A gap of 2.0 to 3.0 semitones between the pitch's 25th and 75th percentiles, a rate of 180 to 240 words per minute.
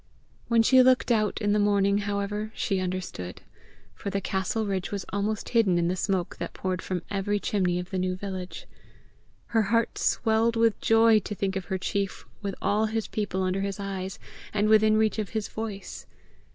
Yes: narrow, 2.4 semitones; average, 190 wpm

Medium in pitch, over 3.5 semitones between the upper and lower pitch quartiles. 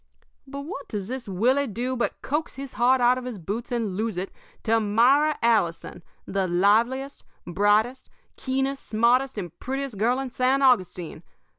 No: high, 240 Hz; average, 4.3 semitones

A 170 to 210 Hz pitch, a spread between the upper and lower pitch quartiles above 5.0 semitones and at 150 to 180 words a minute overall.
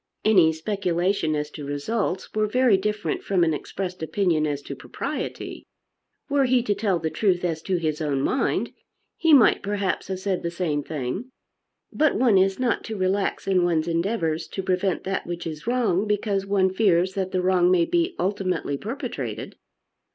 No: medium, 185 Hz; average, 3.7 semitones; average, 175 wpm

